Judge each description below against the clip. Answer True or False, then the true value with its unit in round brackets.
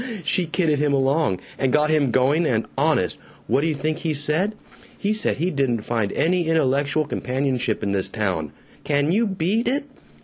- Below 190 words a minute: True (175 wpm)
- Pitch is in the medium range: True (145 Hz)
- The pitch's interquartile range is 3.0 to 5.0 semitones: True (4.0 semitones)